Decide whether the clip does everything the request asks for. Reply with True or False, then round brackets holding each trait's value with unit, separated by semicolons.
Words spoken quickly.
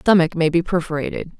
False (170 wpm)